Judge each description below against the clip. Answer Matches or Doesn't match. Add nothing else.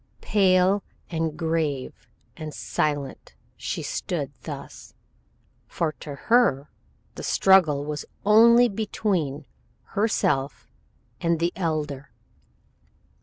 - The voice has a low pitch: Doesn't match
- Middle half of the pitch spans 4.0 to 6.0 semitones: Matches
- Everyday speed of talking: Doesn't match